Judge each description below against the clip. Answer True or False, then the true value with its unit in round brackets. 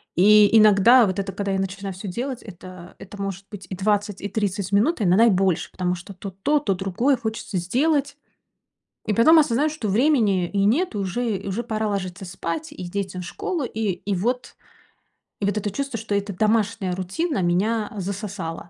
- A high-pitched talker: True (205 Hz)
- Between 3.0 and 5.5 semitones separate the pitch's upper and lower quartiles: True (3.3 semitones)